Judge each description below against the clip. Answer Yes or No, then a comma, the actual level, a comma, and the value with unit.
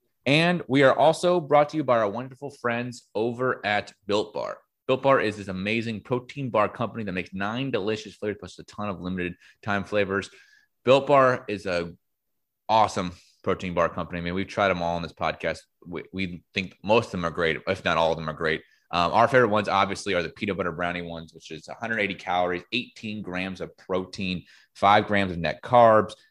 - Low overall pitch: Yes, low, 105 Hz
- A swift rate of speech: Yes, fast, 210 wpm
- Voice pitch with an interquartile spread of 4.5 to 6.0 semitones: Yes, average, 5.2 semitones